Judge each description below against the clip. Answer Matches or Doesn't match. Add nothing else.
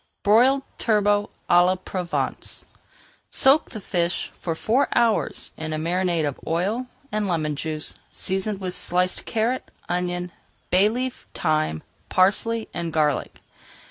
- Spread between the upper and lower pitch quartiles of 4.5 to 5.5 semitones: Doesn't match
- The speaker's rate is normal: Doesn't match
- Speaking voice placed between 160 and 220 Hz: Matches